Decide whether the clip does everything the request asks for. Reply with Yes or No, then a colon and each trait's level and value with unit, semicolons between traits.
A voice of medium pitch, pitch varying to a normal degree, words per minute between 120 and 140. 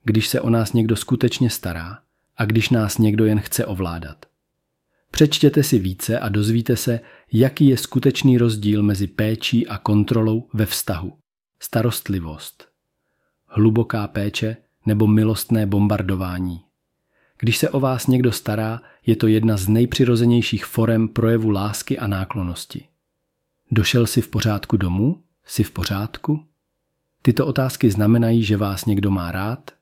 No: low, 115 Hz; average, 3.1 semitones; average, 135 wpm